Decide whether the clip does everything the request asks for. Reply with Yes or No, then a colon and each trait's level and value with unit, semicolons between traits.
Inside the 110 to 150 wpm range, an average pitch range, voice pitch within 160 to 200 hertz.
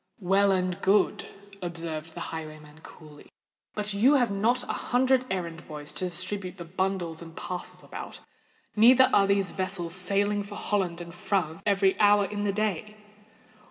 No: average, 160 wpm; average, 3.4 semitones; high, 190 Hz